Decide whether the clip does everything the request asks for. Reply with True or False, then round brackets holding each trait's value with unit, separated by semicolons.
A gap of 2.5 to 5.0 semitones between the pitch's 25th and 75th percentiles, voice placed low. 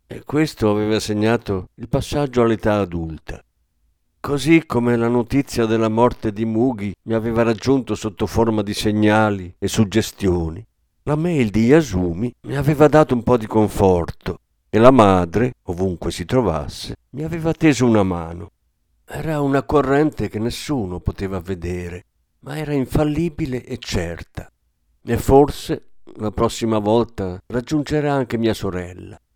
False (5.6 semitones; 110 Hz)